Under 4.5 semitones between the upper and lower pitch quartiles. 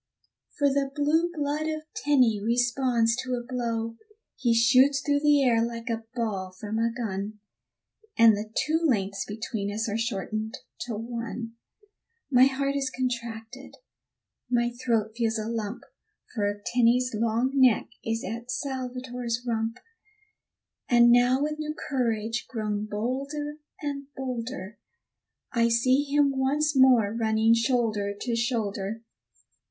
Yes: average, 2.9 semitones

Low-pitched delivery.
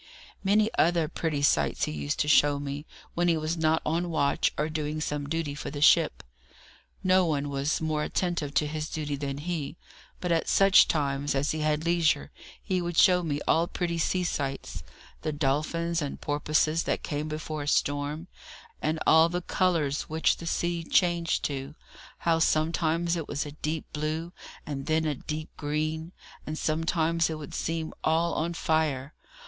No: medium, 155 Hz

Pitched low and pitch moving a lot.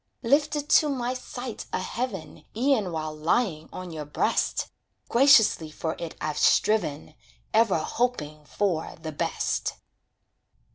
No: high, 195 Hz; wide, 7.9 semitones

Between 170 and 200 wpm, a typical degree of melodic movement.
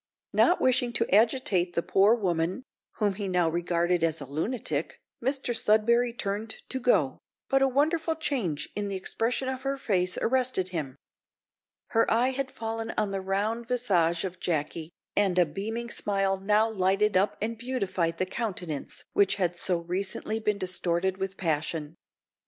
No: average, 160 wpm; average, 4.9 semitones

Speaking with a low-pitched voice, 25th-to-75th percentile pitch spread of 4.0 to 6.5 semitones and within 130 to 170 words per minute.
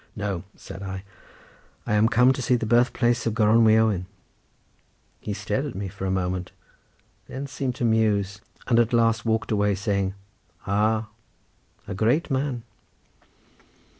No: low, 110 Hz; average, 3.0 semitones; average, 150 wpm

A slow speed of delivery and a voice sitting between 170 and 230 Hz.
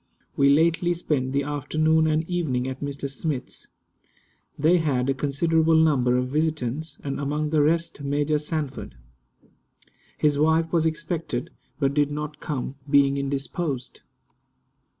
No: slow, 130 wpm; medium, 150 Hz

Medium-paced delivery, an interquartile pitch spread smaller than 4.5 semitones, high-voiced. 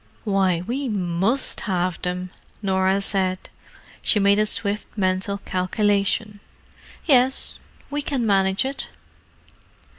No: slow, 100 wpm; average, 2.9 semitones; high, 200 Hz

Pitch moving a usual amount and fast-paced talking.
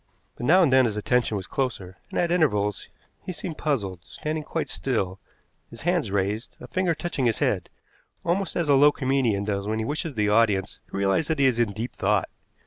No: wide, 7.0 semitones; fast, 210 wpm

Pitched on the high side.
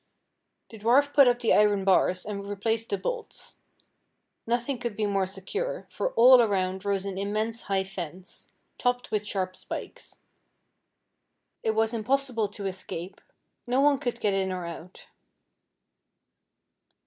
Yes: high, 210 Hz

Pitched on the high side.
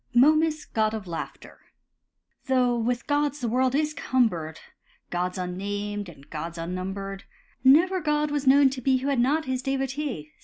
Yes: very high, 250 Hz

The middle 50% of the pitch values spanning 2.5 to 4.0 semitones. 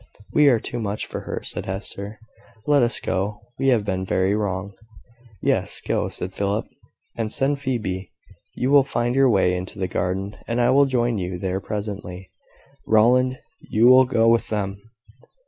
No: average, 4.4 semitones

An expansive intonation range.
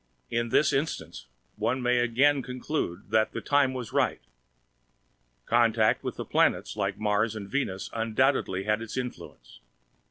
No: average, 3.4 semitones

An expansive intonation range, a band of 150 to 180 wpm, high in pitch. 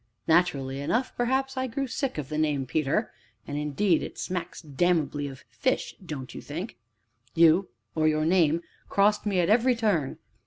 No: wide, 6.2 semitones; average, 170 wpm; medium, 170 Hz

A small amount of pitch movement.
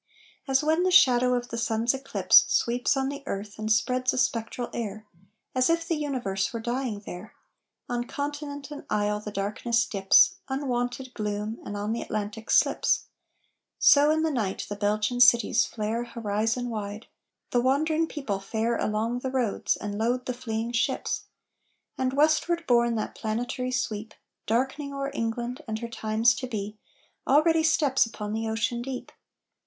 No: average, 3.6 semitones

